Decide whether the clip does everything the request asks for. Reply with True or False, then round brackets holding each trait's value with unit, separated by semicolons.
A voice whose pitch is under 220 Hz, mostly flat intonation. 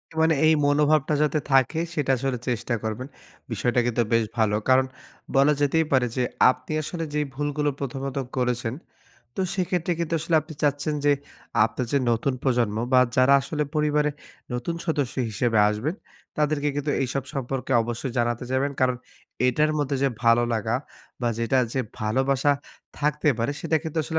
False (135 Hz; 3.6 semitones)